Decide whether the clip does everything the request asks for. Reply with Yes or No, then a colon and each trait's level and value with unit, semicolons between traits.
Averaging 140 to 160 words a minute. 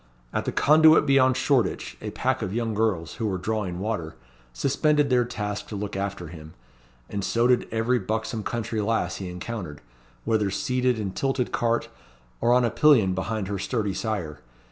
No: average, 175 wpm